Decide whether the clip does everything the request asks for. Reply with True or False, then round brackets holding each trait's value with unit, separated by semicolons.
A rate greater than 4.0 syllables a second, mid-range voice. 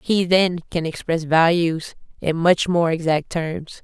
False (3.9 syllables/s; 170 Hz)